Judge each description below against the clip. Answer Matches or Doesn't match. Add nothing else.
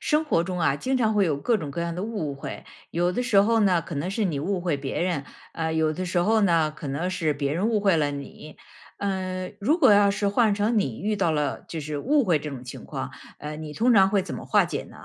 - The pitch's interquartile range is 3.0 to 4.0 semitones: Doesn't match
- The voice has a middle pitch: Matches